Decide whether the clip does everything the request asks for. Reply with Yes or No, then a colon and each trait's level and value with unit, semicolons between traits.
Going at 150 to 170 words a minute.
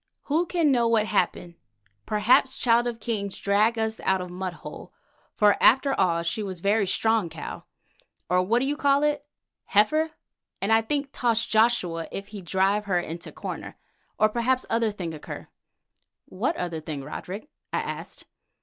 Yes: average, 165 wpm